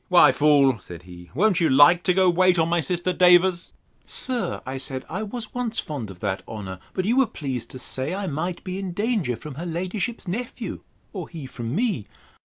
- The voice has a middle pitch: Yes, medium, 175 Hz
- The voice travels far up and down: Yes, wide, 6.3 semitones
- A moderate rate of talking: No, fast, 210 wpm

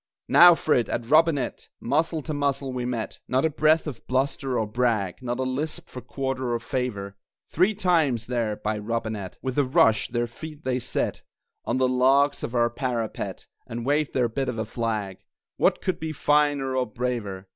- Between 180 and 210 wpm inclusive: Yes, average, 190 wpm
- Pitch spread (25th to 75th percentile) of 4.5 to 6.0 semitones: No, average, 3.6 semitones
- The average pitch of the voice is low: Yes, low, 125 Hz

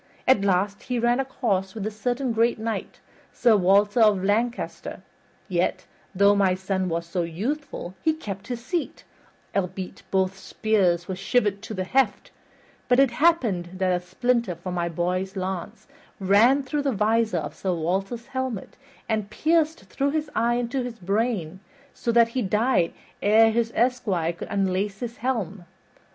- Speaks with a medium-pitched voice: No, high, 210 Hz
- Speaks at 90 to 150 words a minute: No, average, 165 wpm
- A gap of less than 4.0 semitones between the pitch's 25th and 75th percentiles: No, average, 4.5 semitones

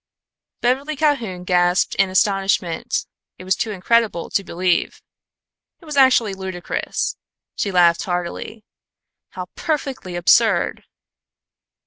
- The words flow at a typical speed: No, slow, 105 wpm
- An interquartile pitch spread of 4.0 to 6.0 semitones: Yes, average, 5.1 semitones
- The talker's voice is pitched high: Yes, high, 195 Hz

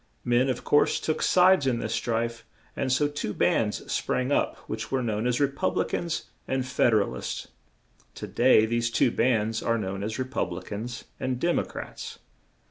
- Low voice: Yes, low, 120 Hz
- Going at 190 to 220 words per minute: Yes, fast, 205 wpm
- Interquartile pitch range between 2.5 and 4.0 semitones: Yes, average, 3.0 semitones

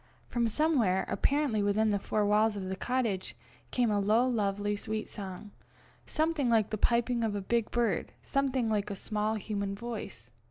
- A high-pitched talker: Yes, high, 215 Hz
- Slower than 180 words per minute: Yes, average, 170 wpm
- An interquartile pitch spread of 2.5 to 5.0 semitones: Yes, average, 2.8 semitones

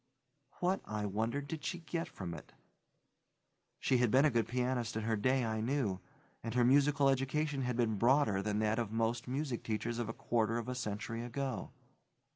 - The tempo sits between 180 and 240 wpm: Yes, average, 190 wpm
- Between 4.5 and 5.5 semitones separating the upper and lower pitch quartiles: No, average, 3.5 semitones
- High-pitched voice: No, low, 120 Hz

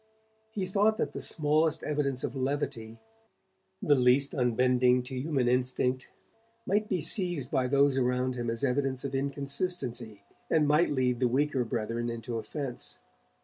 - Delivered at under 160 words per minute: Yes, average, 145 wpm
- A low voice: Yes, low, 130 Hz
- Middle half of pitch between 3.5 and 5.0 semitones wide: No, average, 3.0 semitones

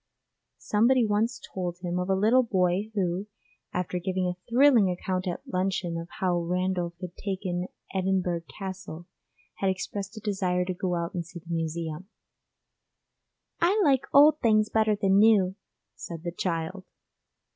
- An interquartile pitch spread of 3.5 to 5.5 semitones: No, average, 2.8 semitones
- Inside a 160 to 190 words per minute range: No, average, 150 wpm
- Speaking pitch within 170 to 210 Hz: Yes, medium, 185 Hz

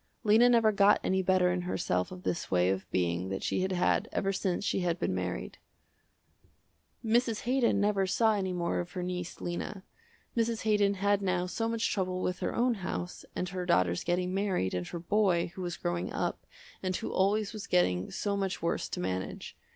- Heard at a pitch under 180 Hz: No, medium, 185 Hz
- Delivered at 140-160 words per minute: No, average, 195 wpm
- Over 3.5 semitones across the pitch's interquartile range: No, average, 2.9 semitones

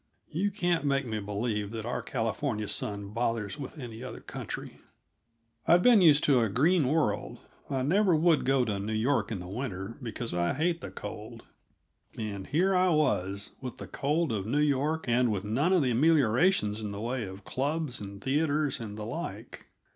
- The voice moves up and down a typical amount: No, wide, 6.4 semitones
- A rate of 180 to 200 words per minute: Yes, average, 185 wpm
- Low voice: Yes, low, 125 Hz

